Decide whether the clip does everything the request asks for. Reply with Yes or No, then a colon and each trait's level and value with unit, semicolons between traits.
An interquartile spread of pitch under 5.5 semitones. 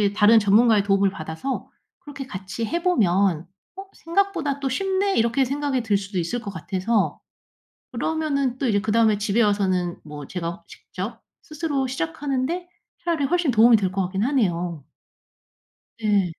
No: wide, 6.4 semitones